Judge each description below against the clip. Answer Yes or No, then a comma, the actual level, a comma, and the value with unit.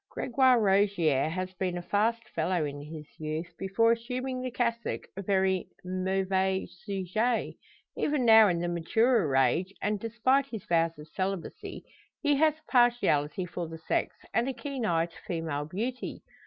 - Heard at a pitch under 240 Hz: Yes, high, 190 Hz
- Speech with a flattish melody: No, wide, 5.6 semitones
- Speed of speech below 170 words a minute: Yes, average, 160 wpm